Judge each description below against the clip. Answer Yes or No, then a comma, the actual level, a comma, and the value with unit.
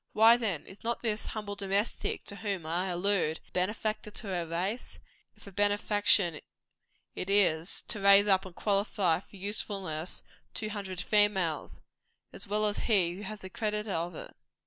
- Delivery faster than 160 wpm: Yes, average, 170 wpm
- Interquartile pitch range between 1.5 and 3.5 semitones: Yes, narrow, 2.6 semitones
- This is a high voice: Yes, high, 200 Hz